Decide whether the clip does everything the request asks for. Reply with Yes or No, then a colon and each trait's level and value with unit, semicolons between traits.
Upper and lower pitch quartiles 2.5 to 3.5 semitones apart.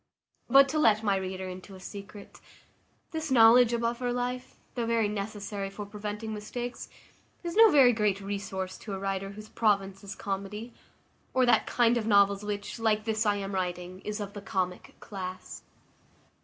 Yes: average, 2.9 semitones